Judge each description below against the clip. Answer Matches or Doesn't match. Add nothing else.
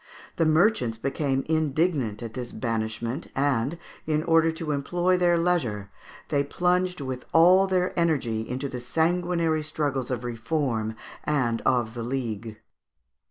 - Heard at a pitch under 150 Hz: Matches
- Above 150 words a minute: Doesn't match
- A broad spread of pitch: Matches